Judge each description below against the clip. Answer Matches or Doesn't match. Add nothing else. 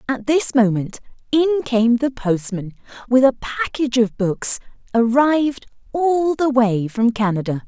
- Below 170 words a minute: Matches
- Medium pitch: Doesn't match